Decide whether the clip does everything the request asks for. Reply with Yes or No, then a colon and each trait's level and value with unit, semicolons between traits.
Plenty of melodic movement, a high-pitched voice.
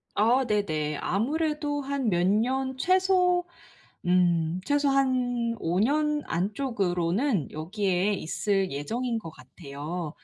Yes: wide, 7.5 semitones; high, 215 Hz